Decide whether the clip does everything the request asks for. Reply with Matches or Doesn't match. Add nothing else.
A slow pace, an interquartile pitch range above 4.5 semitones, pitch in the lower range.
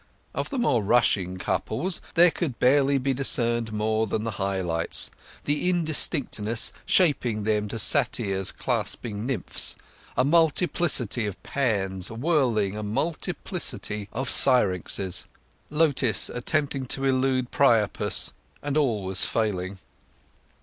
Matches